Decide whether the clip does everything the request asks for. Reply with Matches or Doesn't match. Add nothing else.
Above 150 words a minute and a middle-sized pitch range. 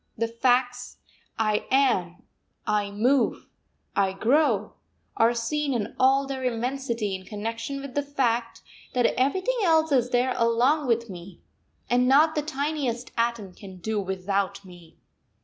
Doesn't match